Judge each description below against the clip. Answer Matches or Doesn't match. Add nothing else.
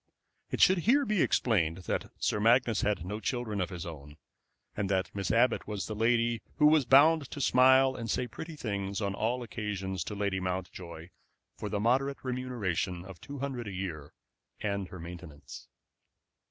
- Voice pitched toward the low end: Matches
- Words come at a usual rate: Matches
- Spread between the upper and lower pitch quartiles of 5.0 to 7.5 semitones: Matches